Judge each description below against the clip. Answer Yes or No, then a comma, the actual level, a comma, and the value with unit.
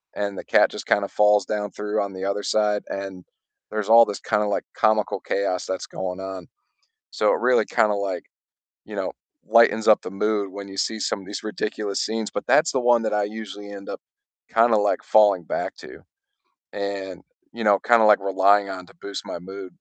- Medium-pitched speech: No, low, 100 Hz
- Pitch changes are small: Yes, narrow, 1.7 semitones